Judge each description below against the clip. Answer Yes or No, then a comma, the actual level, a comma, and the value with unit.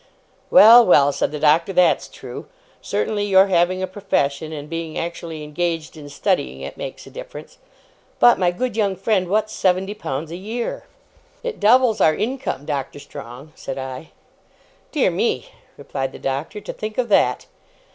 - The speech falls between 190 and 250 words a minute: No, average, 165 wpm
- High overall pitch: No, medium, 175 Hz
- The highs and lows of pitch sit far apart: Yes, wide, 6.0 semitones